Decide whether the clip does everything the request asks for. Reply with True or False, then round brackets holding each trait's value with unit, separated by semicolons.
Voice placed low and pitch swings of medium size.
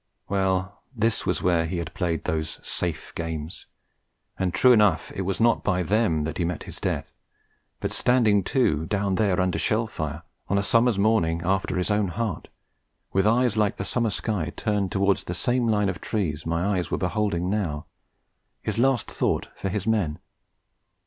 True (95 Hz; 3.8 semitones)